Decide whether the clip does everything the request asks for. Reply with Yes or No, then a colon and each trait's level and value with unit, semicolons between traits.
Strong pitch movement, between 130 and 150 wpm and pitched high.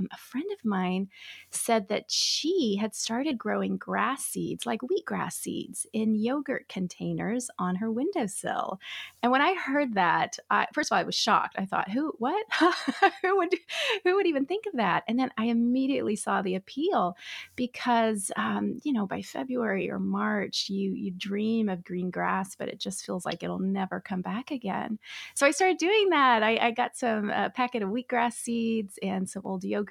No: wide, 5.8 semitones; average, 190 wpm; high, 230 Hz